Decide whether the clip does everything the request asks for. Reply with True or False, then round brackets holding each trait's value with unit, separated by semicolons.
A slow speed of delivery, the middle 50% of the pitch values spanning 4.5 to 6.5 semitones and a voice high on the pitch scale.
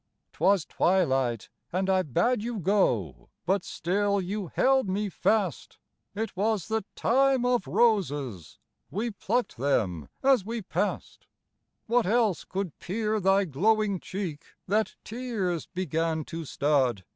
True (130 wpm; 5.3 semitones; 195 Hz)